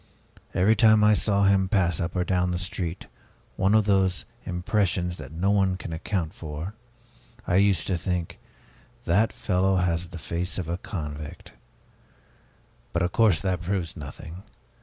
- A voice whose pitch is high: No, very low, 90 Hz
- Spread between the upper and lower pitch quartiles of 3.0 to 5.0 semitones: No, narrow, 2.4 semitones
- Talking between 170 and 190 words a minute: No, average, 160 wpm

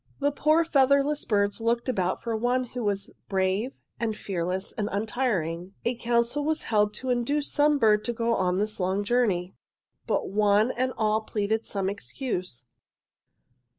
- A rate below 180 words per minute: Yes, average, 155 wpm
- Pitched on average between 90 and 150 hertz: No, high, 220 Hz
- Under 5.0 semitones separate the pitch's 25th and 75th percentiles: Yes, average, 4.0 semitones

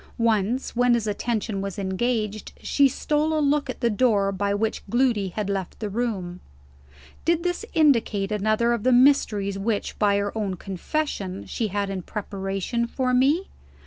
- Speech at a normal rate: Yes, average, 165 wpm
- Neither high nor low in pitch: No, high, 215 Hz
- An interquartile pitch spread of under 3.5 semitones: No, average, 4.1 semitones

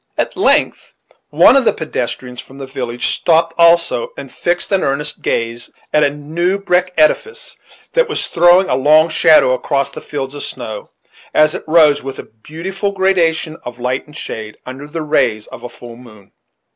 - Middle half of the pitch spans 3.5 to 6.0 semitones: Yes, average, 5.2 semitones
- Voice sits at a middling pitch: Yes, medium, 150 Hz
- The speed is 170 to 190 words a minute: Yes, average, 180 wpm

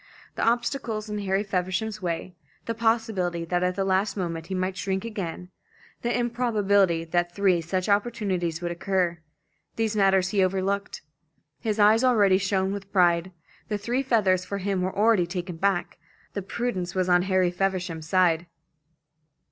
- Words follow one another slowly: No, average, 155 wpm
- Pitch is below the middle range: No, high, 190 Hz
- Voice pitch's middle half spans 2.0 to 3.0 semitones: Yes, narrow, 2.6 semitones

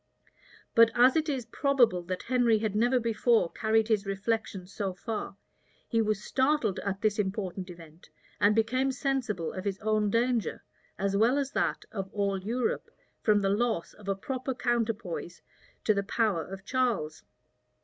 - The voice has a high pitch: Yes, high, 215 Hz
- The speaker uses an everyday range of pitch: Yes, average, 3.6 semitones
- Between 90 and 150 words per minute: No, average, 160 wpm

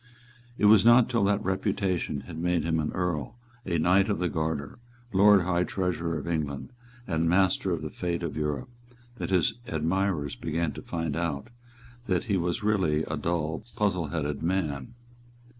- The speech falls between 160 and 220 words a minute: Yes, average, 165 wpm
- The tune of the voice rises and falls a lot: No, average, 3.4 semitones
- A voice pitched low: Yes, very low, 85 Hz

